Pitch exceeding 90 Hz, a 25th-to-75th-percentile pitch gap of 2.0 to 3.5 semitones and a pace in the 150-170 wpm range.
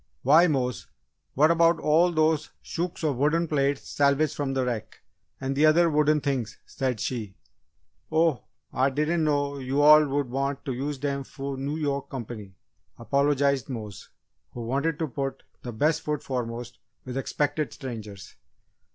Yes: medium, 140 Hz; average, 2.9 semitones; average, 155 wpm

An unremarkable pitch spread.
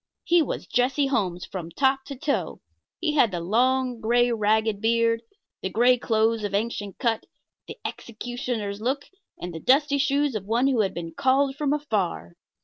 Yes: average, 4.5 semitones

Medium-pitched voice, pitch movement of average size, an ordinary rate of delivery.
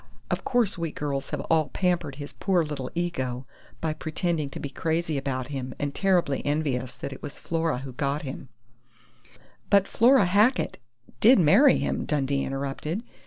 Yes: medium, 150 Hz; average, 4.3 semitones; average, 165 wpm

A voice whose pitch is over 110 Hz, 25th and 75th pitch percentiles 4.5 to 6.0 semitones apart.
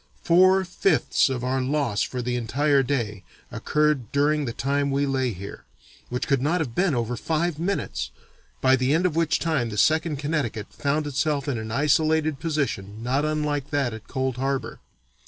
No: medium, 140 Hz; average, 3.7 semitones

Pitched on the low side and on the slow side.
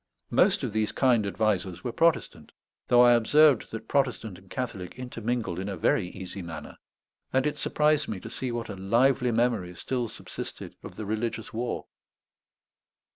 No: low, 115 Hz; average, 165 wpm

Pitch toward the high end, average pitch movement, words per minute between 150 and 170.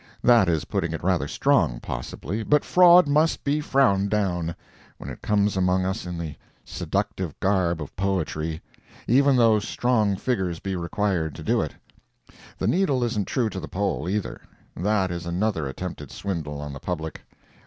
No: very low, 95 Hz; average, 4.6 semitones; average, 165 wpm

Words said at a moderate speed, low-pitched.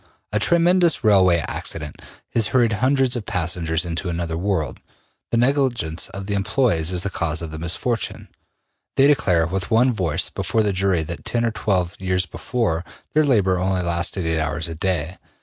Yes: average, 175 wpm; very low, 95 Hz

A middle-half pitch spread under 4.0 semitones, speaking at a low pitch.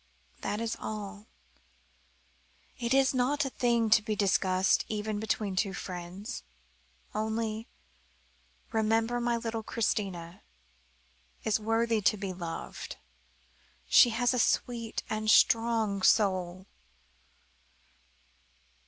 No: narrow, 2.6 semitones; high, 215 Hz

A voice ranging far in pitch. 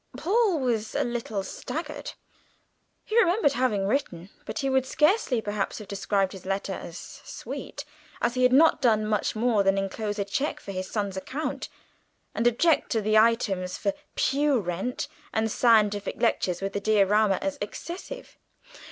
No: average, 5.0 semitones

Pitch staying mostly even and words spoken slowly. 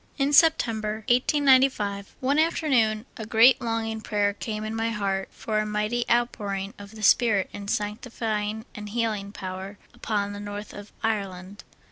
No: narrow, 2.3 semitones; average, 150 wpm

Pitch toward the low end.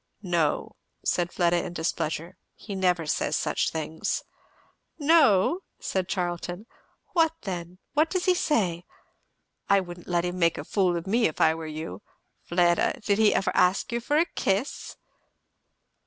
No: medium, 180 Hz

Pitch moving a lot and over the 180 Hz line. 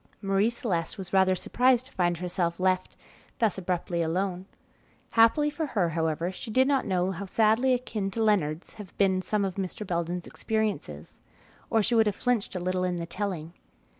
No: average, 3.7 semitones; high, 190 Hz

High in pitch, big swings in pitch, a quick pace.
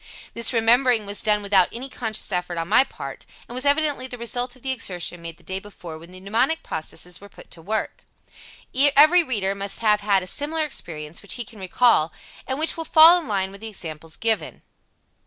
Yes: high, 215 Hz; wide, 5.8 semitones; fast, 210 wpm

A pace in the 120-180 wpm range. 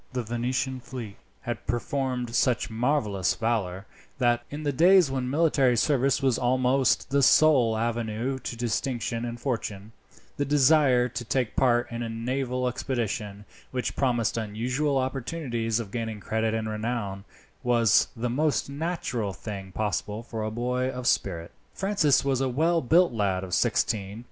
Yes: average, 155 wpm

